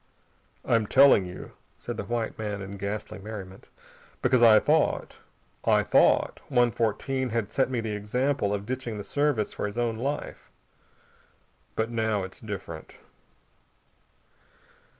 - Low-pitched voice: Yes, low, 110 Hz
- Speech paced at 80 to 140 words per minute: Yes, slow, 135 wpm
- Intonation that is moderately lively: Yes, average, 3.1 semitones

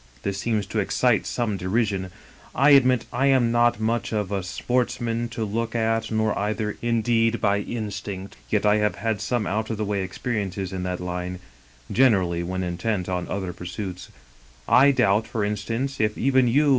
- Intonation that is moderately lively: Yes, average, 3.5 semitones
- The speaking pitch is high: No, low, 110 Hz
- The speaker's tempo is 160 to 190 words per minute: Yes, average, 180 wpm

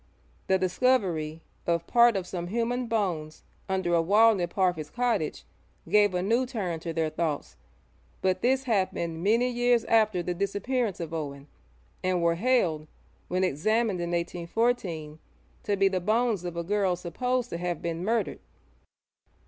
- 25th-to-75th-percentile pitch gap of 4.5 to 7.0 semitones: Yes, average, 5.0 semitones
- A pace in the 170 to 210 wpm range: No, average, 155 wpm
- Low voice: No, medium, 185 Hz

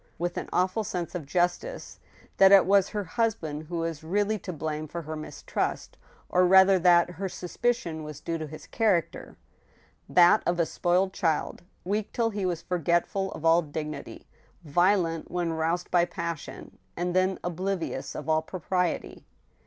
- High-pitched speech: No, medium, 175 Hz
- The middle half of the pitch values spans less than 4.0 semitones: Yes, narrow, 2.6 semitones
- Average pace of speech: Yes, average, 160 wpm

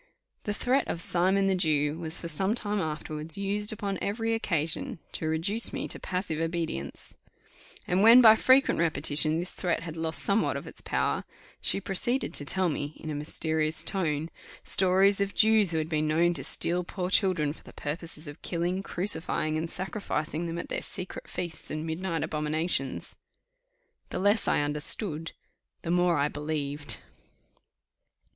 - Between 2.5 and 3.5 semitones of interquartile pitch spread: No, average, 3.9 semitones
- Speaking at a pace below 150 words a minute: No, average, 165 wpm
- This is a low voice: No, medium, 170 Hz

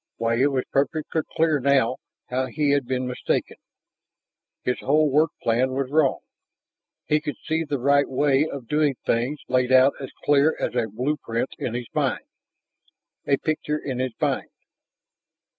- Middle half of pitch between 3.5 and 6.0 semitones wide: No, average, 2.8 semitones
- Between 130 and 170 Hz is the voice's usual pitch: Yes, low, 135 Hz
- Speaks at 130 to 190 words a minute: Yes, average, 160 wpm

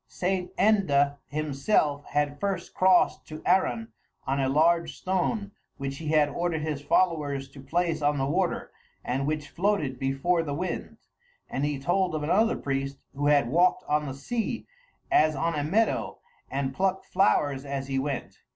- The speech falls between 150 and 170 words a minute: Yes, average, 165 wpm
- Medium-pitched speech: Yes, medium, 150 Hz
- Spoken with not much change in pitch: No, average, 4.4 semitones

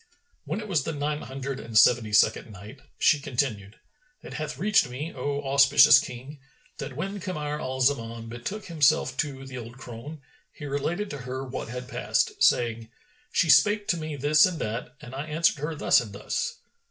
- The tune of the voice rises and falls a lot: No, average, 3.8 semitones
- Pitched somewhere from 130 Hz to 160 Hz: Yes, low, 135 Hz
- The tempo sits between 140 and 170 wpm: No, average, 185 wpm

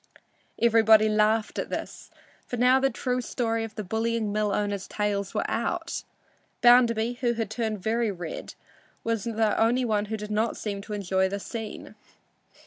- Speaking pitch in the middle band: No, high, 220 Hz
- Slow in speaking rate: No, average, 165 wpm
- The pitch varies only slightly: Yes, narrow, 1.9 semitones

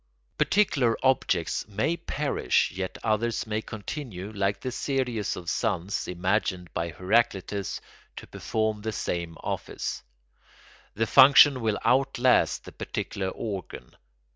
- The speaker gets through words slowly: Yes, slow, 115 wpm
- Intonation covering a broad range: No, average, 4.7 semitones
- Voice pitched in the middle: No, low, 110 Hz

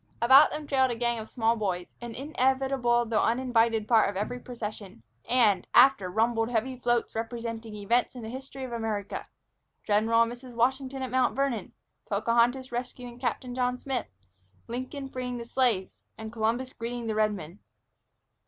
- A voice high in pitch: Yes, high, 240 Hz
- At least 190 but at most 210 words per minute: No, average, 160 wpm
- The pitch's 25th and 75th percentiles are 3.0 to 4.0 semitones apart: No, narrow, 2.4 semitones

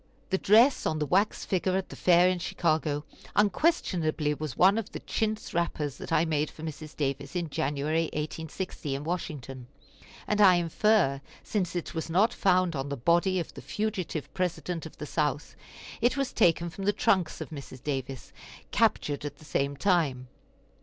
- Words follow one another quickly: No, average, 175 wpm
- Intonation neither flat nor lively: Yes, average, 4.2 semitones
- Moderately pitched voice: Yes, medium, 165 Hz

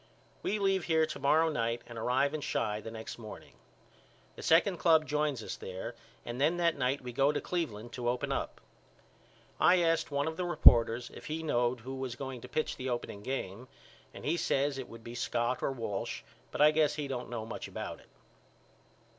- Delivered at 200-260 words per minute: Yes, fast, 205 wpm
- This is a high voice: No, low, 135 Hz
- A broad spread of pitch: No, average, 4.7 semitones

